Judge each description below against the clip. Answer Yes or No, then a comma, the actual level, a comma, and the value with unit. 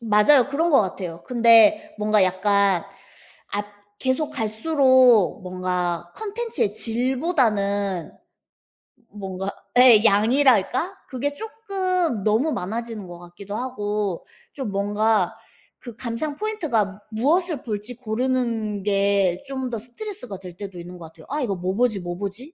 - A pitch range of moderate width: Yes, average, 4.8 semitones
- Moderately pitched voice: No, high, 220 Hz